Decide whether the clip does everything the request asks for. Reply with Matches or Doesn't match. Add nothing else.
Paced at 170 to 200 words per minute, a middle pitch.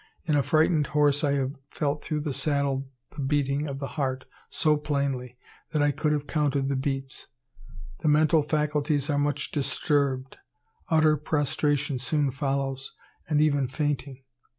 Doesn't match